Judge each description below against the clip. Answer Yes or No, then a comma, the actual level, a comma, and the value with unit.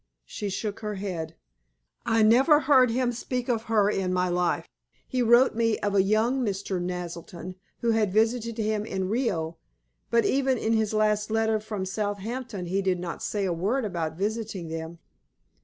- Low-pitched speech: No, high, 210 Hz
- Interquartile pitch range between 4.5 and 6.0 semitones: No, average, 3.7 semitones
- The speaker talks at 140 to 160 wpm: No, average, 175 wpm